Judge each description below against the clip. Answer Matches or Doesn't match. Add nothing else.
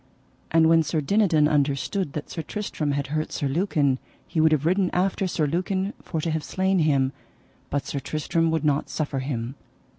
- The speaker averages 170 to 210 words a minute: Matches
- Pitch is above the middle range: Doesn't match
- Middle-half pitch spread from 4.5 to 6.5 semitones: Doesn't match